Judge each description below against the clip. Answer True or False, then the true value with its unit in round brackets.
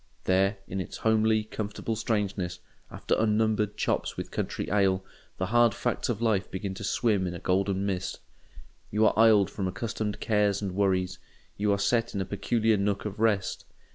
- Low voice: True (100 Hz)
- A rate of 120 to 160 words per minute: False (170 wpm)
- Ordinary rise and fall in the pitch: False (2.3 semitones)